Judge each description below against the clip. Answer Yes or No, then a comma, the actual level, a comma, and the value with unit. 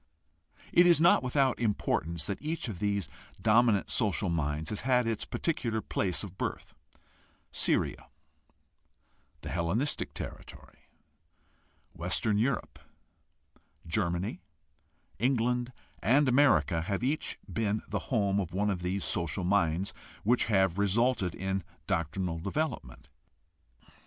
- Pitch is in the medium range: No, low, 100 Hz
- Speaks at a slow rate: Yes, slow, 115 wpm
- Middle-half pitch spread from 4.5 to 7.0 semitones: Yes, wide, 5.4 semitones